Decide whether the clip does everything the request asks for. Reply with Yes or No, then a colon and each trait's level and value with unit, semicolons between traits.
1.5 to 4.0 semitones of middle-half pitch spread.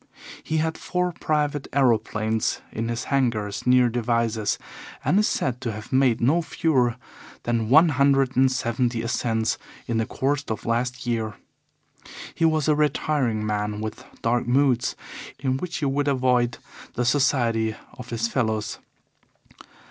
Yes: average, 3.5 semitones